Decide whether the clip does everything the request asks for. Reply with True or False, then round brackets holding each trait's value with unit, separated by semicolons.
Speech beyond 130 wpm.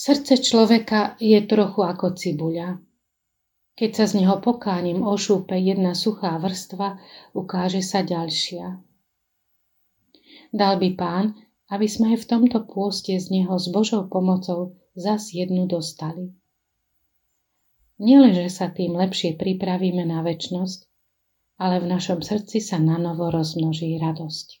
False (120 wpm)